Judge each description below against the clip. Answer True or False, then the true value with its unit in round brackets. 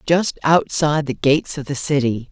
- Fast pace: False (180 wpm)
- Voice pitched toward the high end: False (145 Hz)